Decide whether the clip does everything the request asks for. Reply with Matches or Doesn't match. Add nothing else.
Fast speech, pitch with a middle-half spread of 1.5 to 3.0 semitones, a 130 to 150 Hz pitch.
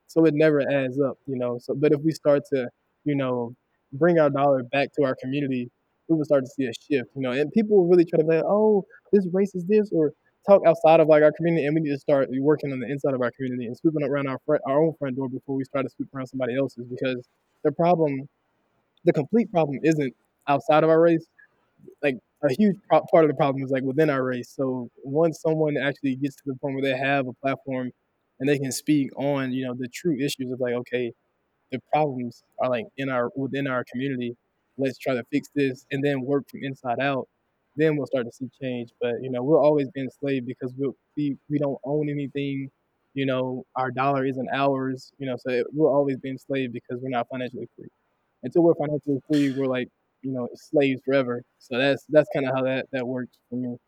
Matches